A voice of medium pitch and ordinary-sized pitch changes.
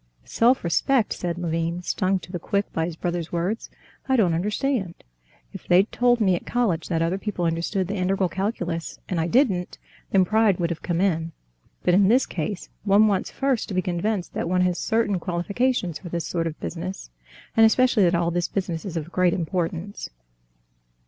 Yes: medium, 180 Hz; average, 3.4 semitones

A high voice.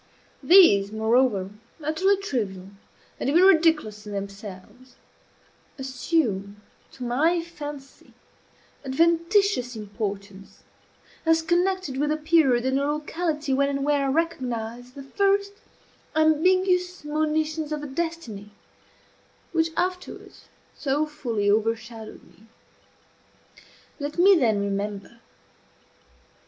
Yes: very high, 280 Hz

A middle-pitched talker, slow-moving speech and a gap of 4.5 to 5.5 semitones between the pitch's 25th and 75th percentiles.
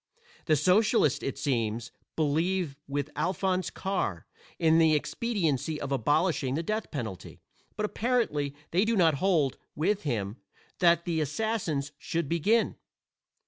Yes: medium, 160 Hz; slow, 130 wpm; average, 5.1 semitones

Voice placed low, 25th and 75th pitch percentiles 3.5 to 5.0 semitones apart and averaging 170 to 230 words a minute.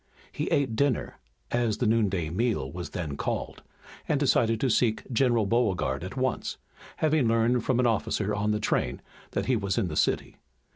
Yes: low, 115 Hz; average, 3.9 semitones; average, 180 wpm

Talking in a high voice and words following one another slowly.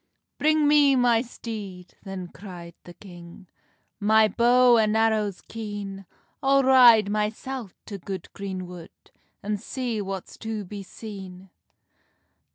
Yes: high, 210 Hz; slow, 125 wpm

